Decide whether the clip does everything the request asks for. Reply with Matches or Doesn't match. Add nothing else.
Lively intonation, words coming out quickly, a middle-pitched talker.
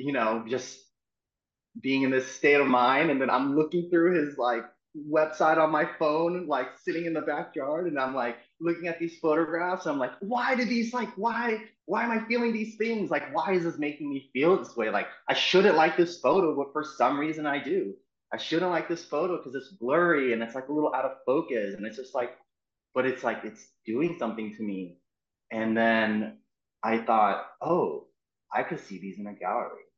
Matches